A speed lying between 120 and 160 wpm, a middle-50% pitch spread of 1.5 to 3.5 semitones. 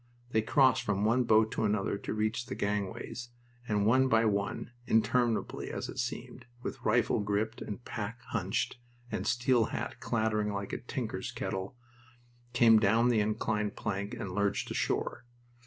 Yes: average, 155 wpm; narrow, 2.5 semitones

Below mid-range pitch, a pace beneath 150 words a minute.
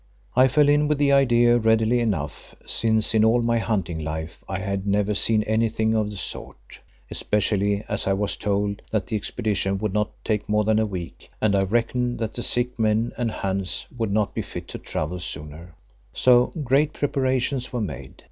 No: low, 110 Hz; average, 190 wpm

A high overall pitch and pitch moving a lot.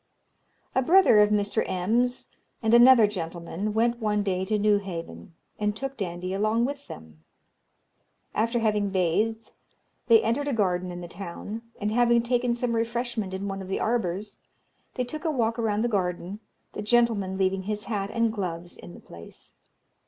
No: high, 210 Hz; average, 3.8 semitones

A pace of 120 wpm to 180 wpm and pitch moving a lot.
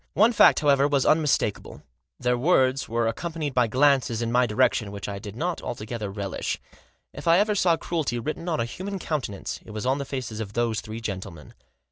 No: average, 195 wpm; wide, 5.7 semitones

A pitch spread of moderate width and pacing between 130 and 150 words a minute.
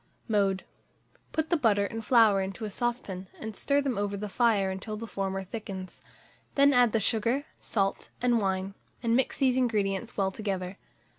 No: average, 3.6 semitones; average, 170 wpm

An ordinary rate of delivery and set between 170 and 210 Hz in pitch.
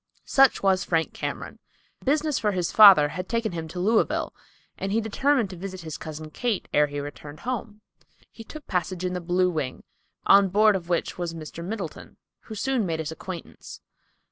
Yes: average, 185 wpm; medium, 185 Hz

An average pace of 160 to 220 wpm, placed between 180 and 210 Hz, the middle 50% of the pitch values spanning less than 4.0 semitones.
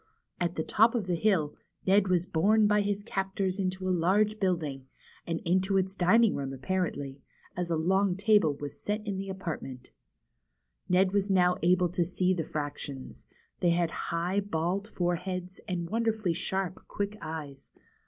Yes: average, 165 wpm; medium, 185 Hz; average, 2.9 semitones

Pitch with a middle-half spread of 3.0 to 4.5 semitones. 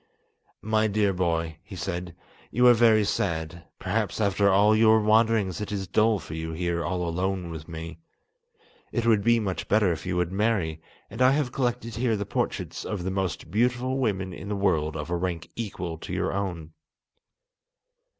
Yes: average, 4.1 semitones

